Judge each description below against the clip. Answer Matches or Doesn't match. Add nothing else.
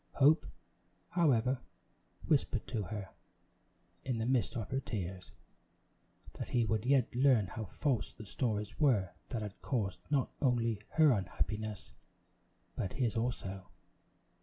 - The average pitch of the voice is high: Doesn't match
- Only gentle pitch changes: Doesn't match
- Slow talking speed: Matches